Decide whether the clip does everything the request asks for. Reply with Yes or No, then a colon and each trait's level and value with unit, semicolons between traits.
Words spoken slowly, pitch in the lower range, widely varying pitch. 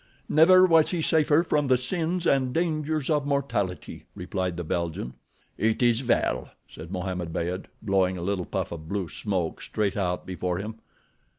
No: average, 165 wpm; low, 105 Hz; wide, 8.5 semitones